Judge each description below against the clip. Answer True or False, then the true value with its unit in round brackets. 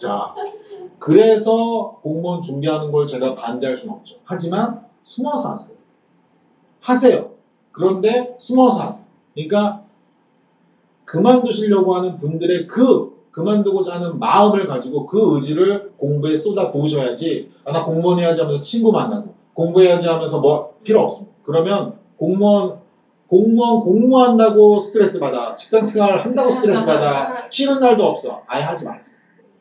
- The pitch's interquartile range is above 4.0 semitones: True (5.6 semitones)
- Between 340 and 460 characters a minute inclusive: False (325 characters per minute)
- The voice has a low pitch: False (200 Hz)